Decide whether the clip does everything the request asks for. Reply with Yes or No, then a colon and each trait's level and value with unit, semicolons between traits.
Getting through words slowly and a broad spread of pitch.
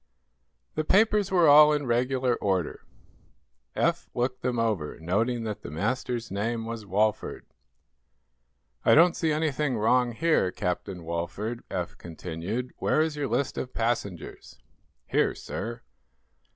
Yes: slow, 130 wpm; wide, 5.7 semitones